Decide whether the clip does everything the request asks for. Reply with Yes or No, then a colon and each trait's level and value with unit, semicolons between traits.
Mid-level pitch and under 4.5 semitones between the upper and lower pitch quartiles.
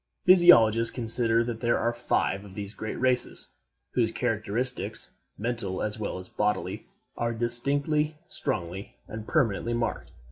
No: low, 115 Hz; average, 2.8 semitones